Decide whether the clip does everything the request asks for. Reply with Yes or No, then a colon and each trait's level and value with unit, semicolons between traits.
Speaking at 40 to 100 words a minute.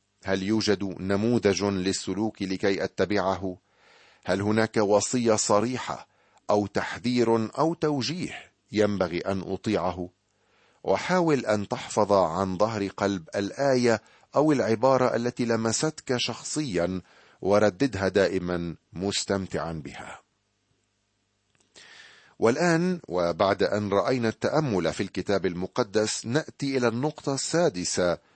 Yes: average, 95 wpm